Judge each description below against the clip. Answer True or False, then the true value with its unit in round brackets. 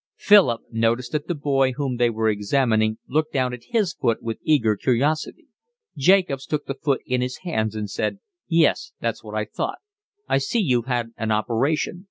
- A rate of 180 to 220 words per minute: True (185 wpm)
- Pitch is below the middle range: True (130 Hz)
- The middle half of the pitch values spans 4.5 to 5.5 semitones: True (4.8 semitones)